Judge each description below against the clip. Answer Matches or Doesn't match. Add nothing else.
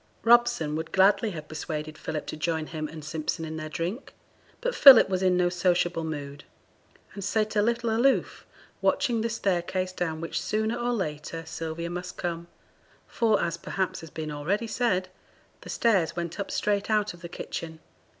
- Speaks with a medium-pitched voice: Matches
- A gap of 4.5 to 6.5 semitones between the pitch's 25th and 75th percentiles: Matches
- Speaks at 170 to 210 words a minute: Matches